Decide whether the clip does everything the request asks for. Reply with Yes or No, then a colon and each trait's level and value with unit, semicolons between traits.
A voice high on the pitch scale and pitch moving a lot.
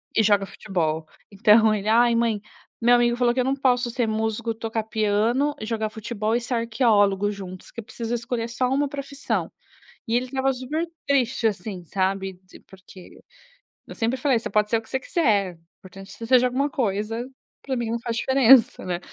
No: high, 230 Hz; average, 3.1 semitones